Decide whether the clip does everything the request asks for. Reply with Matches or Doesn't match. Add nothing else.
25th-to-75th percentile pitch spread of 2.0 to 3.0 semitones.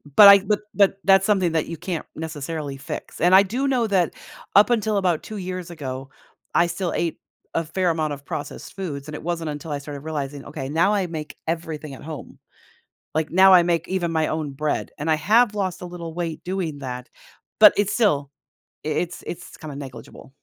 Doesn't match